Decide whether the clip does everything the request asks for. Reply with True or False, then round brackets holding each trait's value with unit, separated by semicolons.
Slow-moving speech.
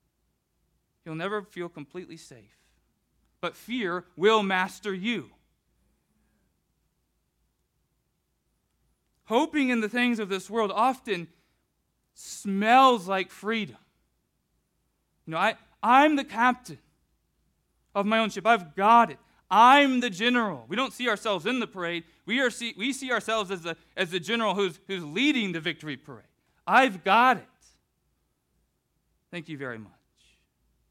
True (130 wpm)